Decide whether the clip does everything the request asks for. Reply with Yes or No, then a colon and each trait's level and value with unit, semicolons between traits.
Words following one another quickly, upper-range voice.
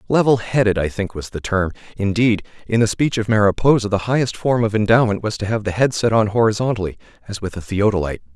No: fast, 215 wpm; low, 105 Hz